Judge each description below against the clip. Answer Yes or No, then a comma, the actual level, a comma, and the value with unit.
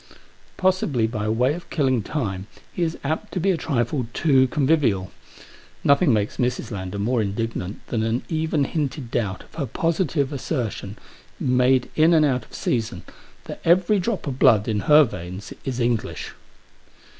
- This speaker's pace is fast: No, average, 160 wpm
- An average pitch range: No, wide, 5.8 semitones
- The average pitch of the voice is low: Yes, low, 130 Hz